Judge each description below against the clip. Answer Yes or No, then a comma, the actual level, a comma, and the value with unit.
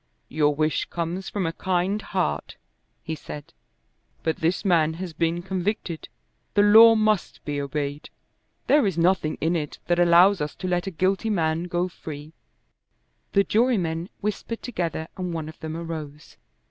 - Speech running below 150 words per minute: No, average, 160 wpm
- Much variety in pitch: No, average, 3.3 semitones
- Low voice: No, medium, 170 Hz